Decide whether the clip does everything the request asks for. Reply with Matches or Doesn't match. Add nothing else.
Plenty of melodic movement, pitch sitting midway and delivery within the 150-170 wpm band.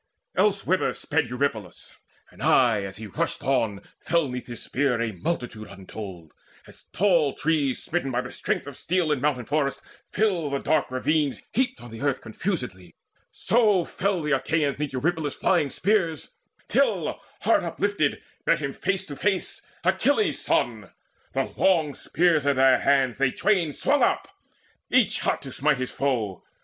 Matches